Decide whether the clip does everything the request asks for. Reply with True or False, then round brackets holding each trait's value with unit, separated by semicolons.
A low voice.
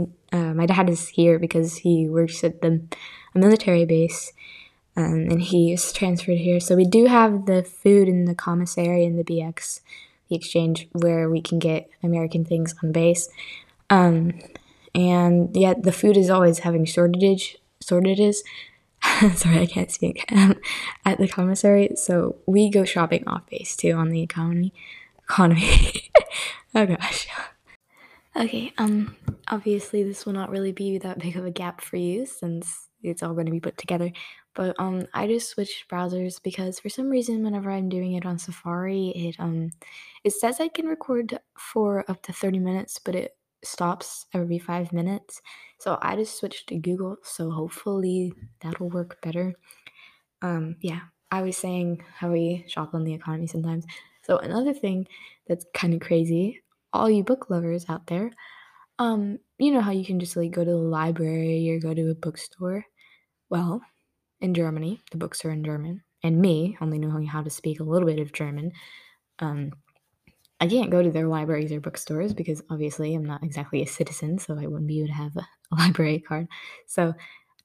False (175 Hz)